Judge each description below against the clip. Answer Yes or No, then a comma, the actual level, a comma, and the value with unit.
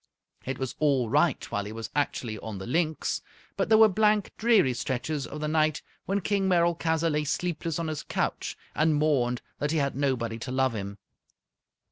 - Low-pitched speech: No, medium, 150 Hz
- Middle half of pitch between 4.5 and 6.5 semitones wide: Yes, average, 4.9 semitones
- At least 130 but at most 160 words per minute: No, average, 185 wpm